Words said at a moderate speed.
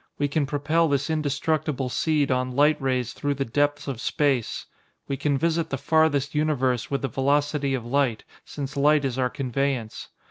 Yes: average, 175 wpm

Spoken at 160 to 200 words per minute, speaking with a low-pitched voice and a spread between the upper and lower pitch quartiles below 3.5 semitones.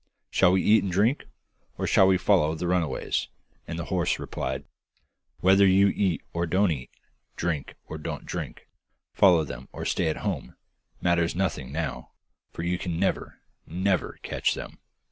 Yes: average, 165 wpm; very low, 90 Hz; average, 2.8 semitones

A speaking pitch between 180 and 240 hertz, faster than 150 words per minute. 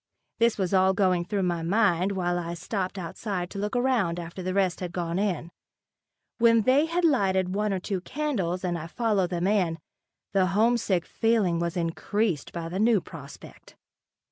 Yes: high, 190 Hz; average, 175 wpm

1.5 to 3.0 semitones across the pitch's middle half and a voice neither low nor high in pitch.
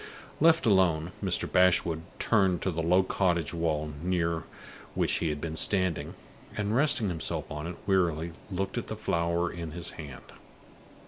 No: narrow, 2.6 semitones; very low, 85 Hz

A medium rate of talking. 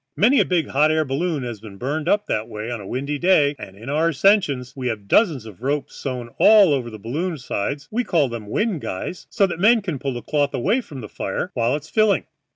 No: fast, 240 wpm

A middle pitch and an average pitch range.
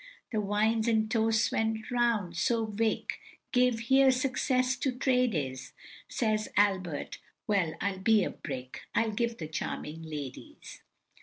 No: high, 220 Hz; average, 4.1 semitones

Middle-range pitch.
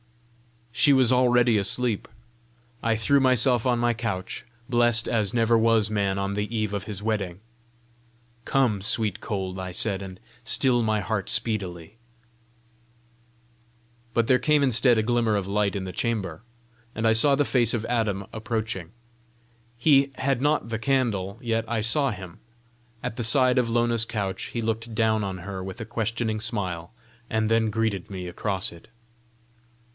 No: low, 110 Hz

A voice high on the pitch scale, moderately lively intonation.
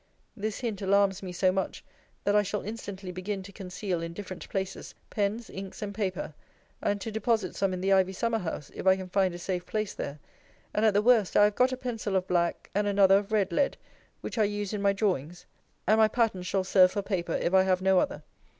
No: high, 195 Hz; narrow, 2.2 semitones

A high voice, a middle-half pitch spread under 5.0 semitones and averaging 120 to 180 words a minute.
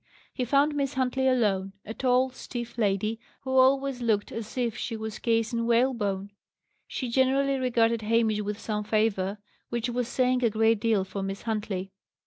Yes: high, 230 Hz; average, 3.2 semitones; average, 170 wpm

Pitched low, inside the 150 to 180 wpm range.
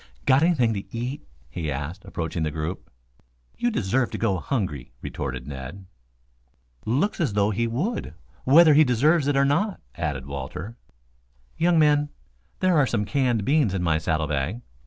Yes: low, 115 Hz; average, 160 wpm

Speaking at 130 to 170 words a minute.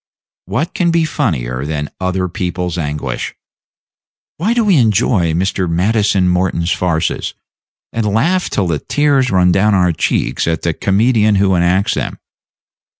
Yes: average, 145 wpm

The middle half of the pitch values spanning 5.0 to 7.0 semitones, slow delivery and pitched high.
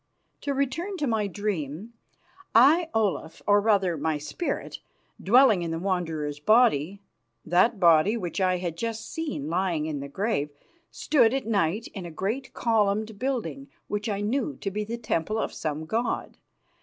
No: wide, 5.6 semitones; average, 160 wpm; high, 205 Hz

